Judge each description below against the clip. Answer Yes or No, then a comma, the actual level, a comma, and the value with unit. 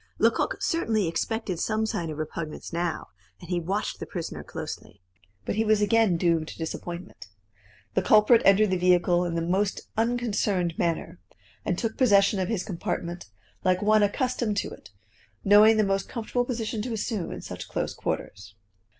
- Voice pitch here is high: Yes, high, 195 Hz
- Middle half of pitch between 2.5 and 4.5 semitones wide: Yes, average, 4.0 semitones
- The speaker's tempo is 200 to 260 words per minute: No, average, 165 wpm